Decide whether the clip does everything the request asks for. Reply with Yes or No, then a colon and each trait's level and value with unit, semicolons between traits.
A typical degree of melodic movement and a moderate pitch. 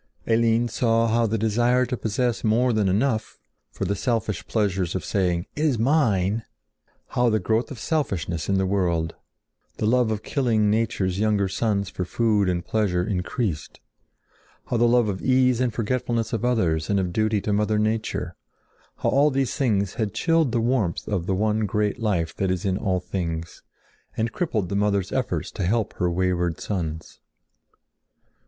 No: average, 3.8 semitones; low, 105 Hz